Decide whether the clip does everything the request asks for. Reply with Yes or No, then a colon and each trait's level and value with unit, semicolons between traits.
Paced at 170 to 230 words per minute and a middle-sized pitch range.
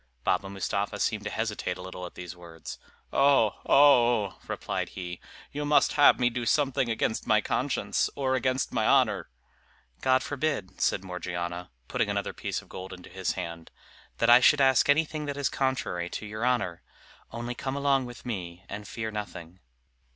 No: average, 175 wpm; wide, 6.4 semitones